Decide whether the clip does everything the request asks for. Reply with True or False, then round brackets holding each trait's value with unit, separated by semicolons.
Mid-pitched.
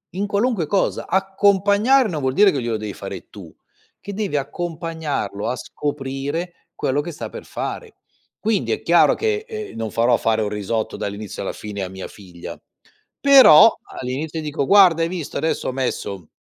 True (155 Hz)